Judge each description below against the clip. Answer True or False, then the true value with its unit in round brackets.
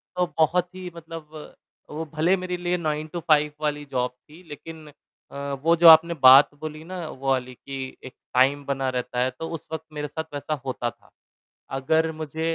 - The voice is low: False (155 Hz)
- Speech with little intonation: False (3.2 semitones)